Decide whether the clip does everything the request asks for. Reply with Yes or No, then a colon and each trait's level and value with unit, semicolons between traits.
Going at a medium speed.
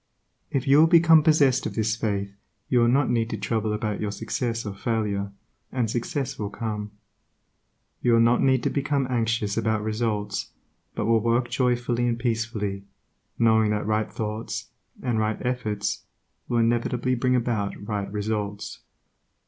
Yes: average, 155 wpm